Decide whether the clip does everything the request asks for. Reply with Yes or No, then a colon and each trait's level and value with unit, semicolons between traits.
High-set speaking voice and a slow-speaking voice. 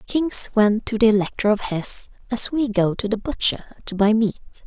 No: high, 220 Hz; fast, 205 wpm